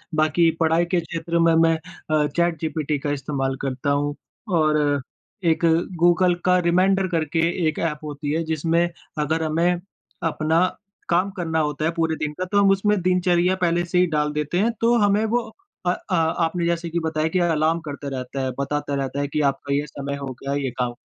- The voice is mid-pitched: Yes, medium, 160 Hz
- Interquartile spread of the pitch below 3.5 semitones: Yes, average, 2.8 semitones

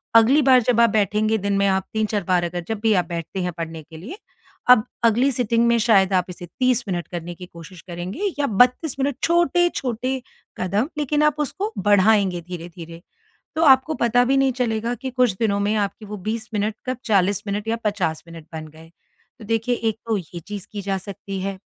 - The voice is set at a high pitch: Yes, high, 210 Hz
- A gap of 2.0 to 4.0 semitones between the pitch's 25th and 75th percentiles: No, average, 5.0 semitones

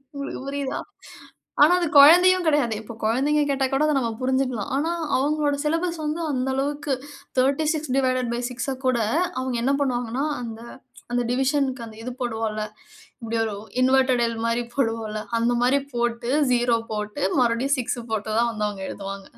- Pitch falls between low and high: No, very high, 255 Hz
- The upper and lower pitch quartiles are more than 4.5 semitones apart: No, average, 3.3 semitones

